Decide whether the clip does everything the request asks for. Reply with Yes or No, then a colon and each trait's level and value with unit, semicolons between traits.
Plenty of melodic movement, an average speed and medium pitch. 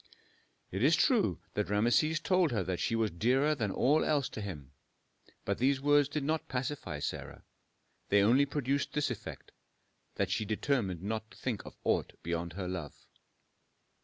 No: wide, 6.5 semitones; average, 165 wpm; low, 120 Hz